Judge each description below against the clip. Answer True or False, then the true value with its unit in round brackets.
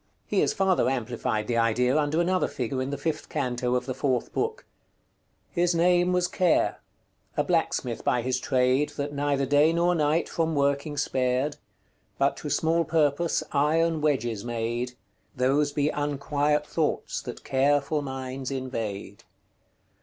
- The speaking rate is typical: True (145 wpm)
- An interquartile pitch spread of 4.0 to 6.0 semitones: False (3.5 semitones)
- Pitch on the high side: False (140 Hz)